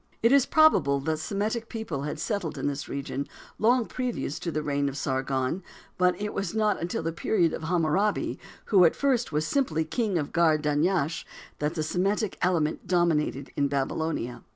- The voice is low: No, medium, 165 Hz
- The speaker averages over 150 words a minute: Yes, average, 175 wpm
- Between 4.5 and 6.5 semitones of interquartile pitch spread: Yes, wide, 5.6 semitones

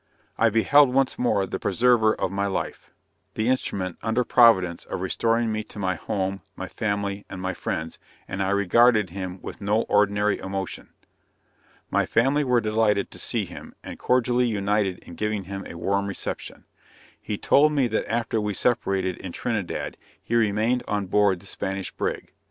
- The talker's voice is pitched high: No, low, 105 Hz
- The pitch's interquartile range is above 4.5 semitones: No, average, 3.1 semitones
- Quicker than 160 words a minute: Yes, average, 170 wpm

